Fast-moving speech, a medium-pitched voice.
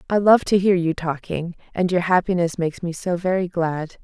Yes: fast, 210 wpm; medium, 175 Hz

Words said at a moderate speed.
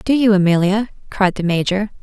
Yes: average, 180 wpm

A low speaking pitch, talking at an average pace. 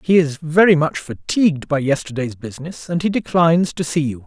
No: medium, 155 Hz; average, 195 wpm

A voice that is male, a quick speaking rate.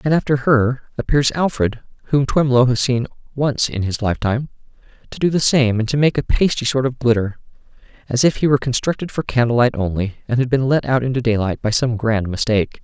Yes: male; fast, 210 wpm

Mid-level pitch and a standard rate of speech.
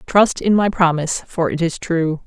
No: medium, 175 Hz; fast, 210 wpm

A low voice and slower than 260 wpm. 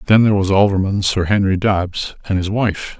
Yes: low, 100 Hz; average, 200 wpm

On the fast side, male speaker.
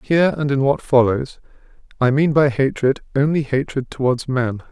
No: average, 165 wpm; male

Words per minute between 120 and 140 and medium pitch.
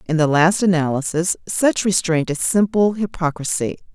Yes: slow, 135 wpm; medium, 175 Hz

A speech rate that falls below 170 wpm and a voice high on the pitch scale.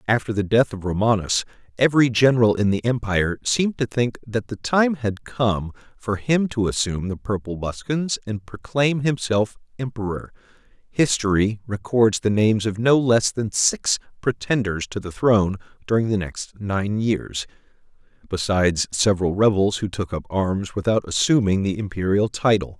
No: average, 155 wpm; low, 110 Hz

